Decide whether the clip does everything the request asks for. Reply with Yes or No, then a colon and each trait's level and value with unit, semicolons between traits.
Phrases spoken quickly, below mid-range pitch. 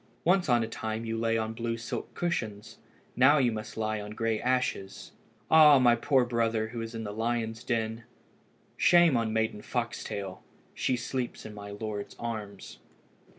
No: average, 170 wpm; low, 115 Hz